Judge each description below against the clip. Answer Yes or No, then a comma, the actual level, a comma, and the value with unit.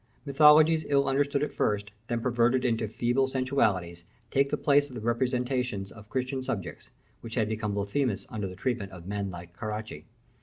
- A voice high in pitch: No, low, 120 Hz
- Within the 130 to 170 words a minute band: No, average, 180 wpm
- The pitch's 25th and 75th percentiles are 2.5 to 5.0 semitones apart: Yes, average, 4.7 semitones